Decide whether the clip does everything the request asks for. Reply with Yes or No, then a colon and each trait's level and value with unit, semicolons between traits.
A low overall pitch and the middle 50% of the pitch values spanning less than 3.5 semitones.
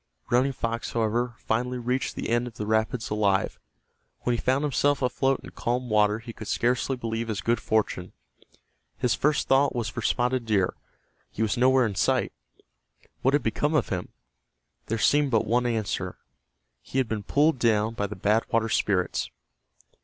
Yes: low, 115 Hz; narrow, 2.6 semitones